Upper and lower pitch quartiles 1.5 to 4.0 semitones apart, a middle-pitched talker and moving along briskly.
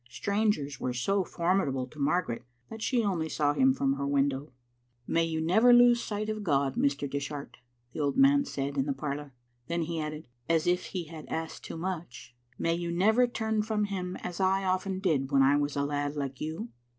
No: wide, 5.5 semitones; medium, 160 Hz; fast, 210 wpm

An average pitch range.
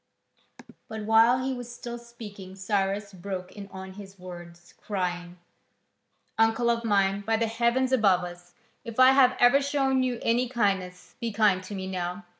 Yes: average, 4.0 semitones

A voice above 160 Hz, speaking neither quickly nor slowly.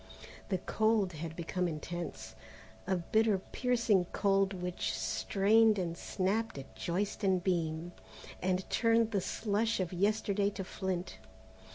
No: high, 190 Hz; slow, 130 wpm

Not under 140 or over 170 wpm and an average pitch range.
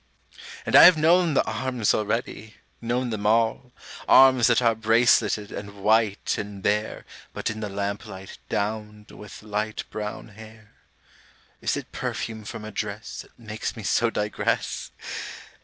No: average, 145 wpm; narrow, 1.8 semitones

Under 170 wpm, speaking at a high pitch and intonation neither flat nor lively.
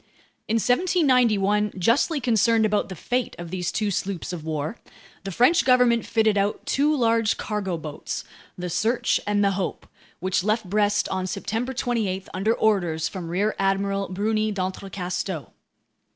Yes: average, 150 wpm; high, 205 Hz; average, 3.5 semitones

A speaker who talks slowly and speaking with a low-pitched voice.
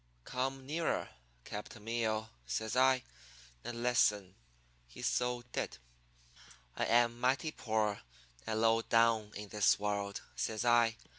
Yes: slow, 125 wpm; low, 115 Hz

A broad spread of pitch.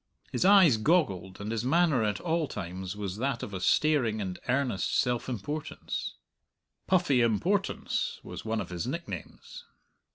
Yes: wide, 7.3 semitones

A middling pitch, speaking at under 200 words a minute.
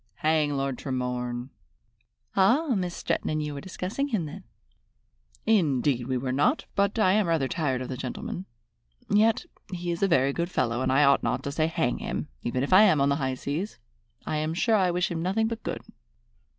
No: medium, 155 Hz; fast, 205 wpm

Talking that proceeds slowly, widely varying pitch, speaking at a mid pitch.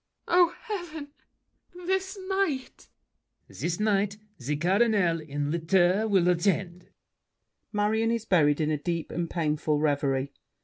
Yes: slow, 125 wpm; wide, 6.5 semitones; medium, 180 Hz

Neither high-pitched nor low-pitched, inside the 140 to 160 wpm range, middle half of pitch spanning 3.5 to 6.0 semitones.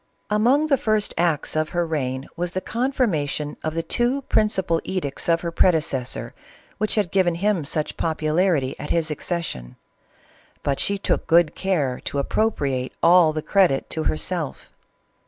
Yes: medium, 165 Hz; average, 155 wpm; average, 4.5 semitones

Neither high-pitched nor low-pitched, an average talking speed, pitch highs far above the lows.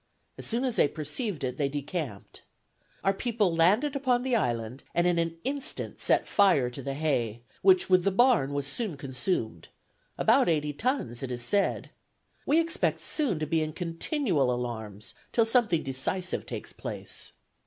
Yes: medium, 165 Hz; average, 165 wpm; wide, 8.8 semitones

